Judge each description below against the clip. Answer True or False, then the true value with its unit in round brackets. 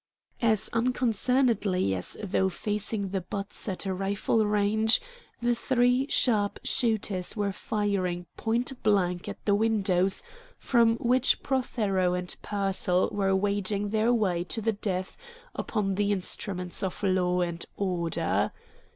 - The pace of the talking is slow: True (130 wpm)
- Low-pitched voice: False (205 Hz)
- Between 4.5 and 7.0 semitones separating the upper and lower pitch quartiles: False (3.1 semitones)